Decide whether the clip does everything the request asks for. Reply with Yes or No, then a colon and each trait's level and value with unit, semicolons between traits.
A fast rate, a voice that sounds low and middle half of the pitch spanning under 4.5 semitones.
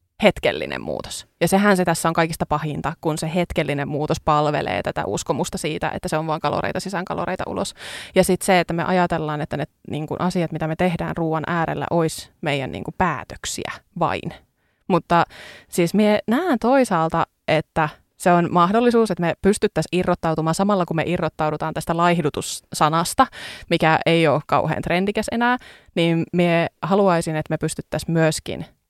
No: fast, 160 wpm; medium, 170 Hz; narrow, 2.5 semitones